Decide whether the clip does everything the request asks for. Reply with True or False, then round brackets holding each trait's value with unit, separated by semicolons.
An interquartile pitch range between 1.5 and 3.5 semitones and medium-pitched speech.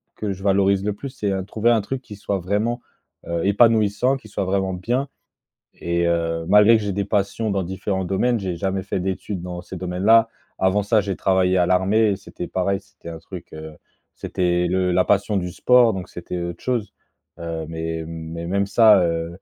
False (2.8 semitones; 95 Hz)